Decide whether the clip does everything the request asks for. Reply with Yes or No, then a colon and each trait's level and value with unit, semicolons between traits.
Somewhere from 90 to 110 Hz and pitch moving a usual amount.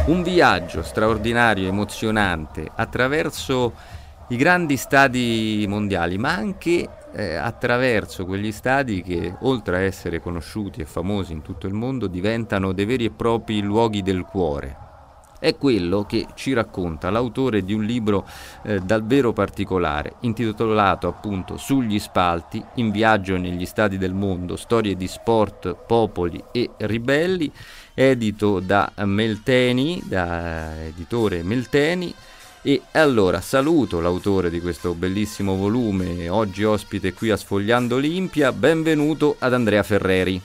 Yes: low, 105 Hz; average, 4.2 semitones